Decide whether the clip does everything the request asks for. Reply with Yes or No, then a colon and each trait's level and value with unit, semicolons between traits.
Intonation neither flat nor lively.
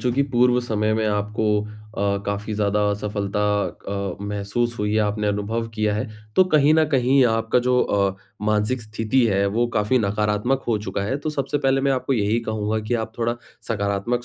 Yes: average, 3.0 semitones